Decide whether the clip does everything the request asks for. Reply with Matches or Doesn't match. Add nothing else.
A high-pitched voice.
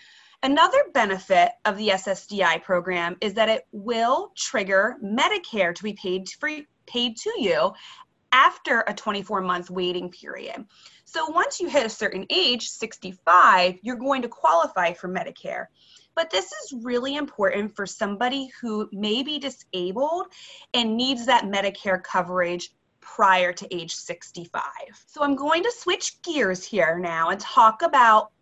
Matches